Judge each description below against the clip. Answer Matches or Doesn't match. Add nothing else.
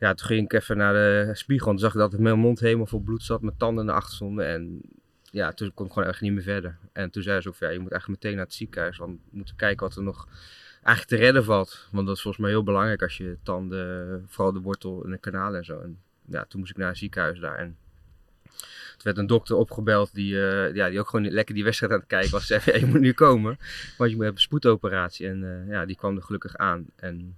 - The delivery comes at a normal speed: Doesn't match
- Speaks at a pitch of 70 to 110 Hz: Matches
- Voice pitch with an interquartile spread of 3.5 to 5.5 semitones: Doesn't match